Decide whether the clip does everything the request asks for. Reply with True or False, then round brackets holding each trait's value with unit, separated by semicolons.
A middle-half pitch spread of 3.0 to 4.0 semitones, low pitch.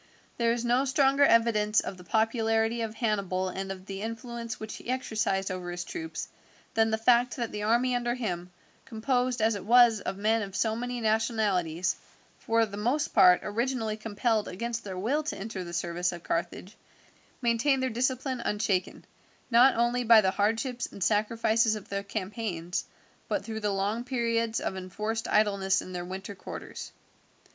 False (3.3 semitones; 220 Hz)